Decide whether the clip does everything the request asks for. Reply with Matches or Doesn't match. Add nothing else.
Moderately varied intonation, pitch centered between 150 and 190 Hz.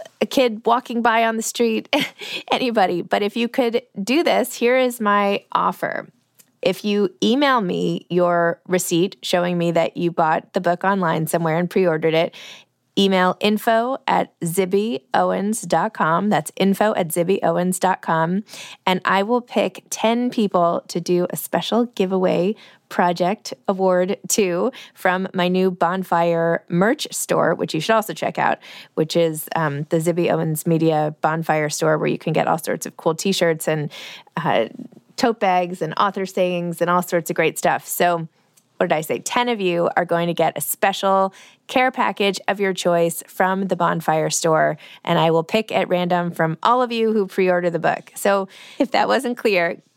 Matches